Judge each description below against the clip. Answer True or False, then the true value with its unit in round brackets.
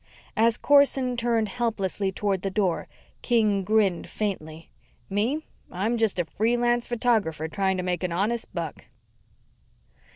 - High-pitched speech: True (210 Hz)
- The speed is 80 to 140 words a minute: True (135 wpm)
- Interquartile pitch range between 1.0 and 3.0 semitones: False (4.1 semitones)